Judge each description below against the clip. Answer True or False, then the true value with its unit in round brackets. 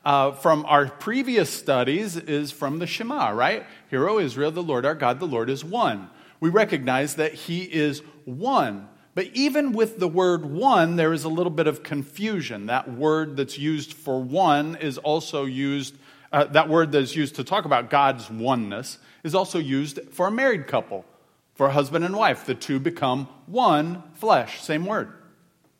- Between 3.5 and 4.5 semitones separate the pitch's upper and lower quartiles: True (3.9 semitones)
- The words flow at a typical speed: True (180 wpm)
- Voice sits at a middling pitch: True (150 Hz)